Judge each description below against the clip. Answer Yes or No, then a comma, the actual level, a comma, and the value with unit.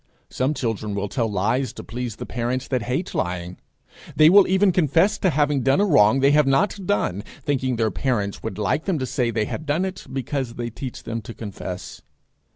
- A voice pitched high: No, low, 130 Hz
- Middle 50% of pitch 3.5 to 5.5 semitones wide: Yes, average, 5.2 semitones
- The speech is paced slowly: No, fast, 205 wpm